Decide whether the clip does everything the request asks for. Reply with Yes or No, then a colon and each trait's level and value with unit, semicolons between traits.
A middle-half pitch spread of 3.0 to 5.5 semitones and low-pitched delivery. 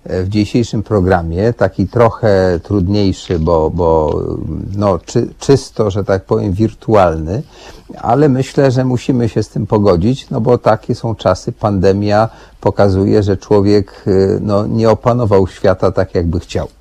Yes: average, 3.5 semitones; low, 105 Hz